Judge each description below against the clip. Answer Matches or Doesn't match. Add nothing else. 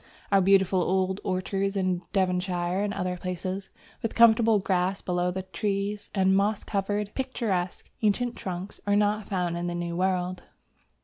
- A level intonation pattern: Matches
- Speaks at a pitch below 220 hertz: Matches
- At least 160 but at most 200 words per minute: Doesn't match